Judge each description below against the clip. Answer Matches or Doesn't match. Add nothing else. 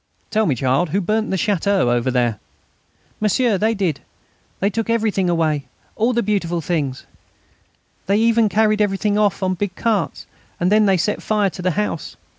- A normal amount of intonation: Matches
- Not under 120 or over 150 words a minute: Doesn't match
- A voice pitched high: Matches